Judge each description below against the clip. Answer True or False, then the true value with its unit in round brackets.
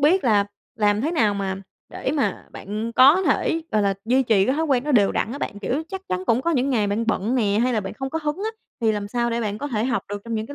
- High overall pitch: True (230 Hz)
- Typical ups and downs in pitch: True (4.9 semitones)